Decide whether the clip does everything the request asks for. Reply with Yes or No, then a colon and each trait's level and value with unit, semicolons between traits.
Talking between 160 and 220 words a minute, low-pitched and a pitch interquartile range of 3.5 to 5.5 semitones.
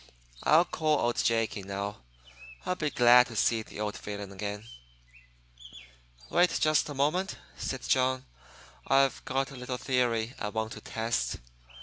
No: average, 150 wpm; low, 125 Hz; average, 4.2 semitones